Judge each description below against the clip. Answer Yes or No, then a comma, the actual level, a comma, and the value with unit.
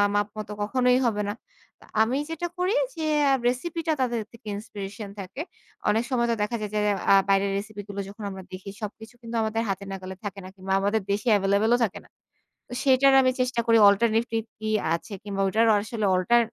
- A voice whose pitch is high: Yes, high, 215 Hz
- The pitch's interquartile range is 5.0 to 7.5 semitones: No, average, 3.1 semitones